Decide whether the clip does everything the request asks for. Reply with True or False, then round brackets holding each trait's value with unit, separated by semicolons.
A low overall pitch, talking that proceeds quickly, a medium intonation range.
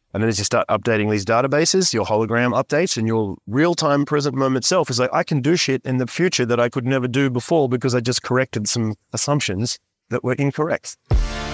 True (125 Hz; 220 wpm; 3.9 semitones)